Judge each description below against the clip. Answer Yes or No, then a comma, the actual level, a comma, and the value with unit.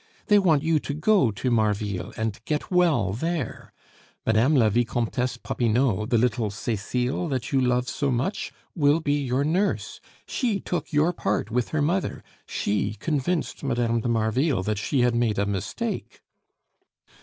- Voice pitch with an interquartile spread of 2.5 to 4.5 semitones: No, wide, 5.5 semitones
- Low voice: Yes, low, 125 Hz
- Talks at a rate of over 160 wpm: No, average, 155 wpm